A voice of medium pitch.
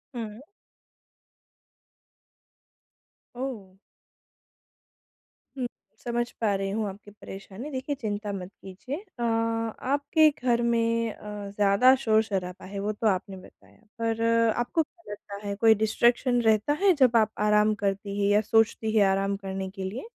No: high, 215 Hz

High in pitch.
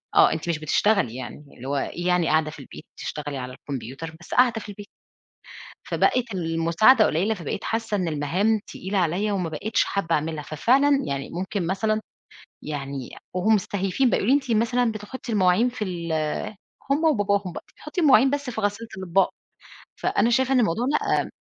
Yes: high, 195 Hz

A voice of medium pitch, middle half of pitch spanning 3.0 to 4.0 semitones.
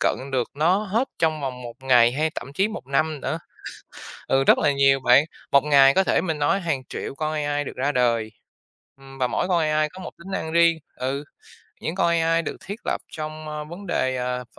Yes: medium, 150 Hz; average, 3.6 semitones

